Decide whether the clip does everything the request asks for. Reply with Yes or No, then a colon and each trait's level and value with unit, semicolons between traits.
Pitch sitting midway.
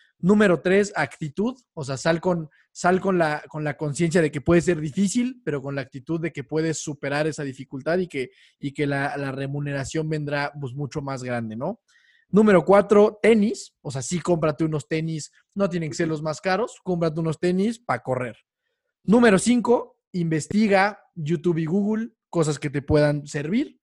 Yes: medium, 165 Hz